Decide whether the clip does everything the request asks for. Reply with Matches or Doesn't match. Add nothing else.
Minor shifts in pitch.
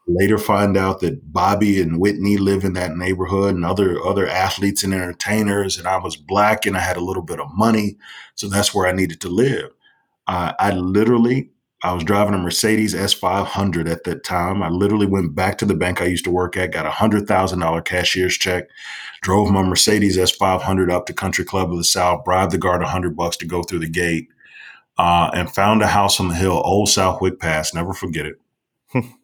Matches